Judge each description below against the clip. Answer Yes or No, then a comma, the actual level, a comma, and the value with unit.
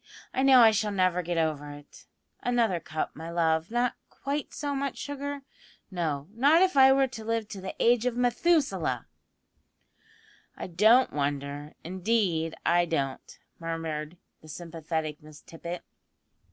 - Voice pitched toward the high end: No, medium, 180 Hz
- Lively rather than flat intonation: Yes, wide, 7.4 semitones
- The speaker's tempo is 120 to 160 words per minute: Yes, average, 145 wpm